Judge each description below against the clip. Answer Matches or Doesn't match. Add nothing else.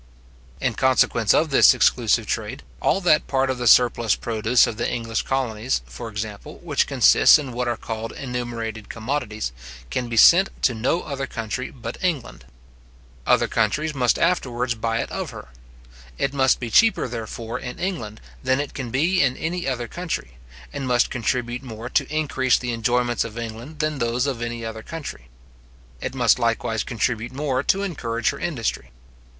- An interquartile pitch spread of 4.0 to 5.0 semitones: Doesn't match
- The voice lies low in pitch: Matches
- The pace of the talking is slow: Doesn't match